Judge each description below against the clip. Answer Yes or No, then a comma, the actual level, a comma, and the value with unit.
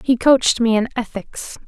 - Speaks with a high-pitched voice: Yes, high, 240 Hz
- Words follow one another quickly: No, average, 180 wpm